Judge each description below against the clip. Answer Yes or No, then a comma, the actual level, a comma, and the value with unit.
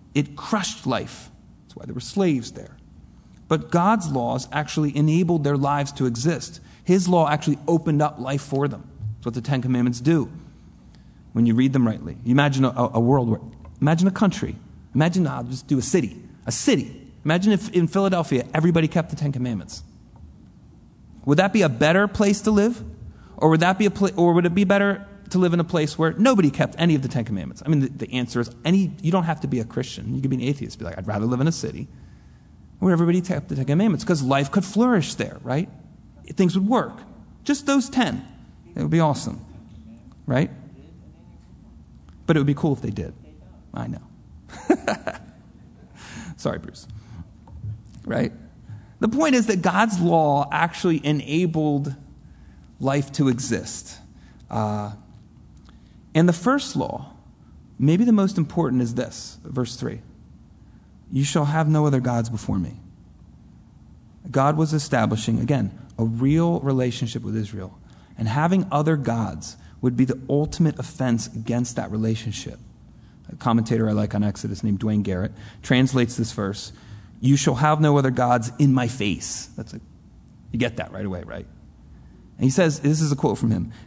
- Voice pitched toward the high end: No, low, 135 Hz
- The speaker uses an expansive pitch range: Yes, wide, 6.6 semitones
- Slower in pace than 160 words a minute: No, average, 180 wpm